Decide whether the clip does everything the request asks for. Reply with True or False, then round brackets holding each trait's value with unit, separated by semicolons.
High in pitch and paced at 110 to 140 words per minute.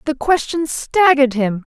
True (285 Hz; 135 wpm)